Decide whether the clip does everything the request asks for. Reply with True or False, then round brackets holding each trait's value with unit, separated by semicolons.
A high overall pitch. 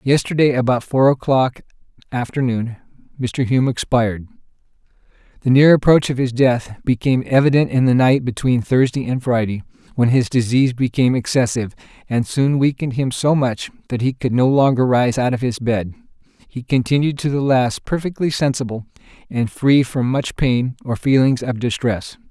False (130 Hz)